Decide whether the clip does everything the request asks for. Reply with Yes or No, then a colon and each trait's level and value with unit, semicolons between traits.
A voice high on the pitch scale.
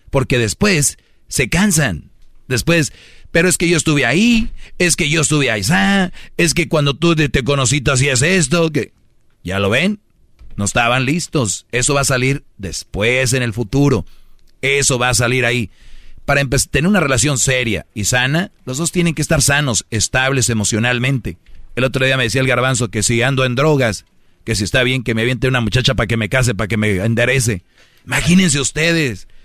No: low, 130 Hz